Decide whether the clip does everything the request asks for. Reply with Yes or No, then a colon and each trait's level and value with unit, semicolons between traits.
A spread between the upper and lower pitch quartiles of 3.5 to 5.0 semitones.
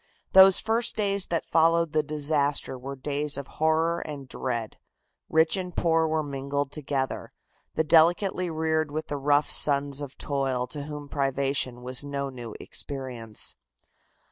No: average, 2.7 semitones